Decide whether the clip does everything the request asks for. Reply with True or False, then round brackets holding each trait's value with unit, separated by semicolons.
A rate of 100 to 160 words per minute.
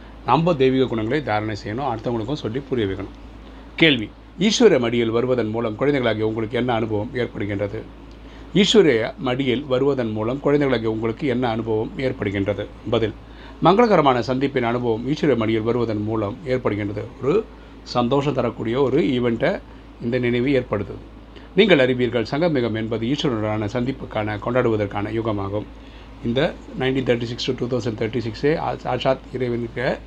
True (130 wpm)